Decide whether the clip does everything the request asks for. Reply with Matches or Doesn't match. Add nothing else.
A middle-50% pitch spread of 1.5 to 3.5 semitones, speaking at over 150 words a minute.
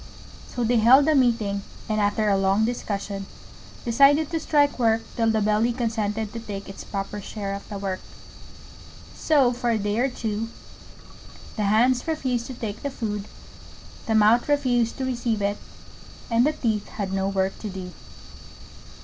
Matches